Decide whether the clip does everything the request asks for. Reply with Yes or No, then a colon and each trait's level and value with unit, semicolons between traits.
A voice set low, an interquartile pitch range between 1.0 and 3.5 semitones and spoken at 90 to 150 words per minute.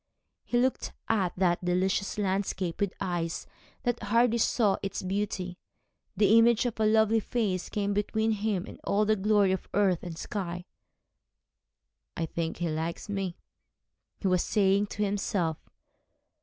No: high, 200 Hz; average, 2.9 semitones; average, 145 wpm